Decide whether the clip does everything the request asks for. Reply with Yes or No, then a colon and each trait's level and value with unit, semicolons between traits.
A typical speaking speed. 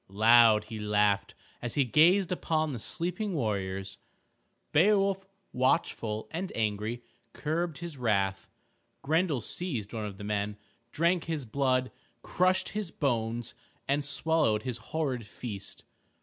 No: slow, 125 wpm